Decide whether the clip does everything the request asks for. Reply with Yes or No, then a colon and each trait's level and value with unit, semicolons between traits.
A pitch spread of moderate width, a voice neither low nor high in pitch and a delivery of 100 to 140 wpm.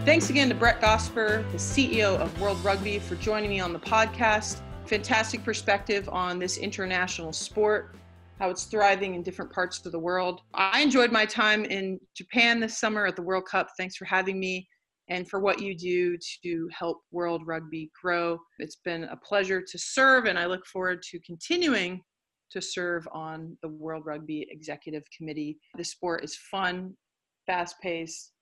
No: average, 3.0 semitones; medium, 180 Hz; average, 175 wpm